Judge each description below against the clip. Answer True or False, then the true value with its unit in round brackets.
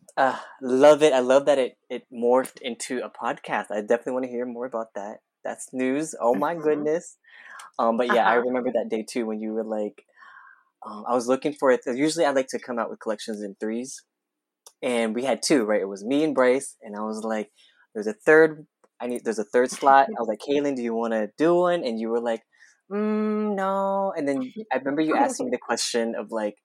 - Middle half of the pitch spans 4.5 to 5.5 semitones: True (5.2 semitones)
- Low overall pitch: True (125 Hz)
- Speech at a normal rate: False (230 wpm)